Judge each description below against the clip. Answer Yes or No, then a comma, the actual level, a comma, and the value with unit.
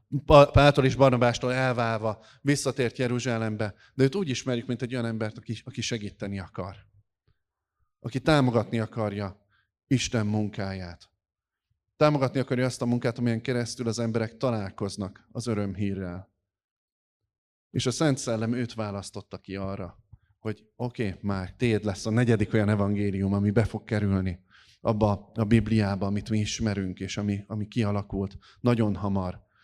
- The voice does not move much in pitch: No, average, 3.3 semitones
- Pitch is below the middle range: Yes, low, 110 Hz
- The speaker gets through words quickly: No, average, 140 wpm